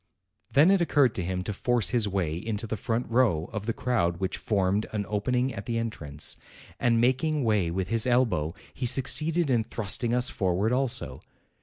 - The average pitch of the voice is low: Yes, low, 115 Hz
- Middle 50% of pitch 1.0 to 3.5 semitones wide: No, average, 4.6 semitones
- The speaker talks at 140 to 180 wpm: No, average, 190 wpm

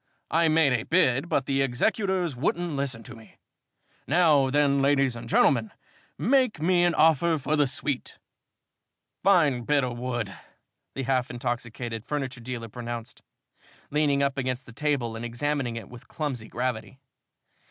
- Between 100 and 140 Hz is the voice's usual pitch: Yes, low, 135 Hz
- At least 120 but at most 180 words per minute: Yes, average, 150 wpm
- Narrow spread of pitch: No, average, 3.8 semitones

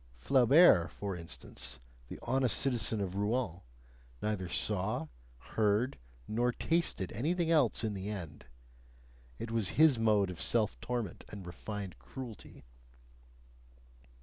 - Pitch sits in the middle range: No, low, 105 Hz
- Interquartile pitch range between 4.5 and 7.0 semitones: Yes, average, 4.8 semitones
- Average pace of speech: No, slow, 120 wpm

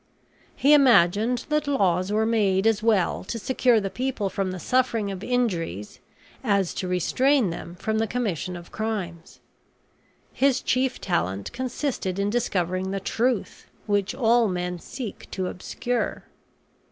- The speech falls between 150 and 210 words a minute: No, average, 140 wpm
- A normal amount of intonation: Yes, average, 4.9 semitones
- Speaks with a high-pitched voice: Yes, high, 210 Hz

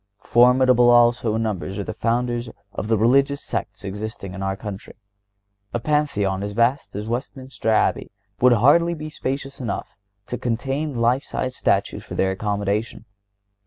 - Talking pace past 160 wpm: No, average, 155 wpm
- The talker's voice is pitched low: Yes, low, 120 Hz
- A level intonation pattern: No, average, 3.8 semitones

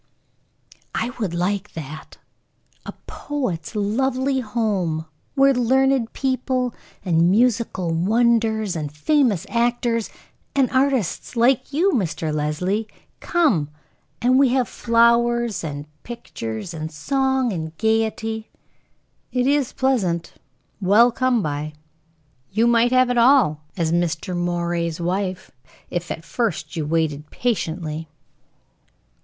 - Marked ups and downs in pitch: Yes, wide, 6.8 semitones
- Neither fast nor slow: No, slow, 115 wpm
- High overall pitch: Yes, high, 220 Hz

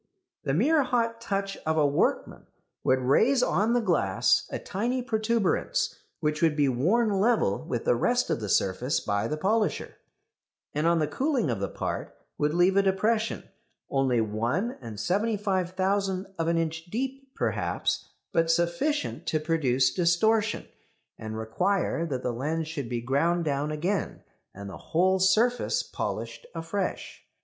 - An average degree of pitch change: No, wide, 7.5 semitones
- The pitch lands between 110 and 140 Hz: No, medium, 170 Hz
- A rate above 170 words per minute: No, average, 150 wpm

